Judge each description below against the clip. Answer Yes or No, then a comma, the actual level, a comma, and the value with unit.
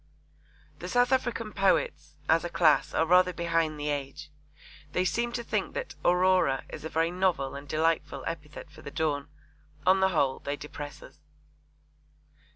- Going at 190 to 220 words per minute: No, average, 165 wpm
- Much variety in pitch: No, average, 3.9 semitones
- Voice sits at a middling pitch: Yes, medium, 165 Hz